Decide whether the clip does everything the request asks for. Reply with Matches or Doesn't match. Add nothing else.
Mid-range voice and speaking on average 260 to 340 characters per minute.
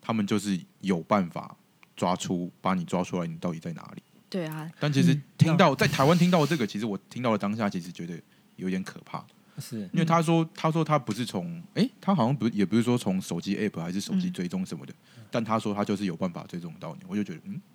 Doesn't match